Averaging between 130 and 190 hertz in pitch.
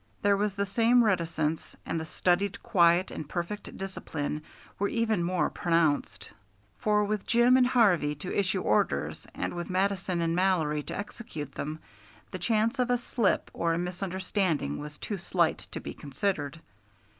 Yes: medium, 185 Hz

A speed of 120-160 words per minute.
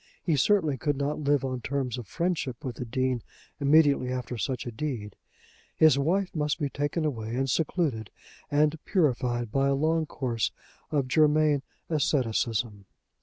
Yes: average, 155 wpm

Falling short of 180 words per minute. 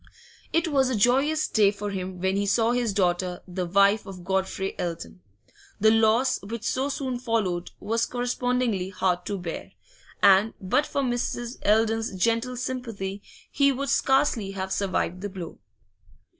Yes: average, 155 wpm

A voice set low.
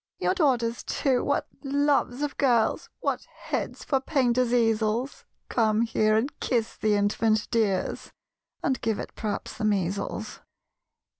No: high, 230 Hz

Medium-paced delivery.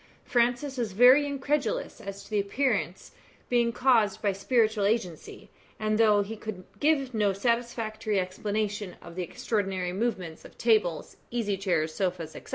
Yes: average, 150 wpm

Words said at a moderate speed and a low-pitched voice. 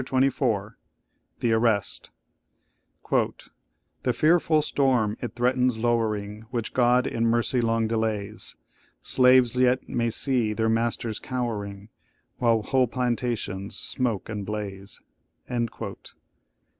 No: slow, 105 wpm; low, 115 Hz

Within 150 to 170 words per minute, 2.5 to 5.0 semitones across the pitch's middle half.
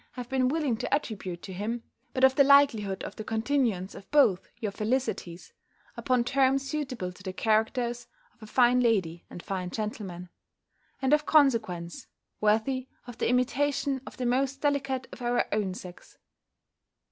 Yes: average, 160 wpm; average, 4.7 semitones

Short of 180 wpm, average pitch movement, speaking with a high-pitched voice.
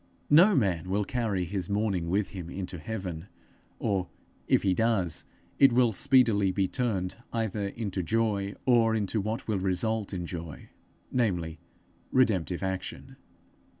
No: average, 140 wpm; average, 3.6 semitones; low, 100 Hz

